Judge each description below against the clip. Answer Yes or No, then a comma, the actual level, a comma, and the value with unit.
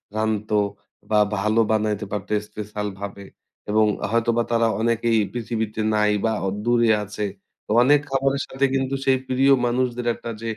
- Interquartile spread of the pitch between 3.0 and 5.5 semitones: No, narrow, 2.4 semitones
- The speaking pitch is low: Yes, low, 115 Hz